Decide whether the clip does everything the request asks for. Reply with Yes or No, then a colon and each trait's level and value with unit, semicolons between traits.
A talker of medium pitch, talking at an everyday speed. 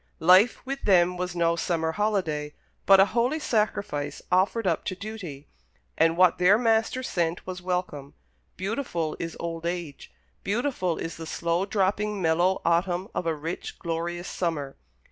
Yes: medium, 180 Hz; average, 150 wpm